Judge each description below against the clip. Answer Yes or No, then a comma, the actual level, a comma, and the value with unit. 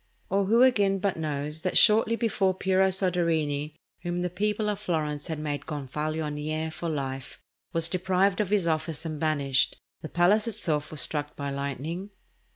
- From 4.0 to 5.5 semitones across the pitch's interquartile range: Yes, average, 4.3 semitones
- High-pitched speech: No, medium, 165 Hz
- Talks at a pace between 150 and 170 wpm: Yes, average, 160 wpm